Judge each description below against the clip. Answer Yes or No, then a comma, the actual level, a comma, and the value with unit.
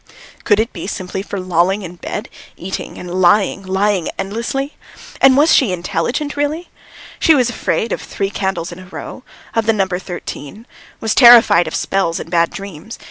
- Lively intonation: No, average, 4.2 semitones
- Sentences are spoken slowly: No, average, 175 wpm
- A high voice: Yes, high, 195 Hz